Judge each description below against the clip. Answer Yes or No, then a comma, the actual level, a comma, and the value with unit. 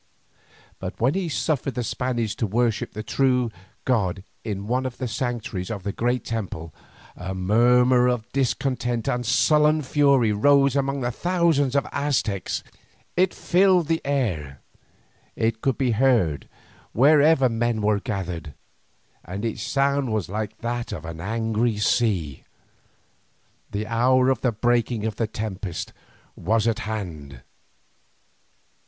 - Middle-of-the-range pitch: No, low, 115 Hz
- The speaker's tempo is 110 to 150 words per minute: Yes, average, 140 wpm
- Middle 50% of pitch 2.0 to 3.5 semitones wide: No, average, 4.3 semitones